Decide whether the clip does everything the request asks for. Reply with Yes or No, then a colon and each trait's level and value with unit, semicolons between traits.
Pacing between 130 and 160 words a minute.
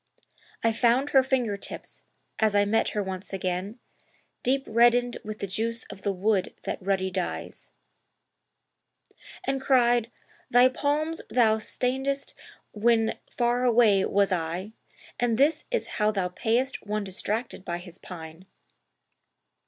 Yes: slow, 135 wpm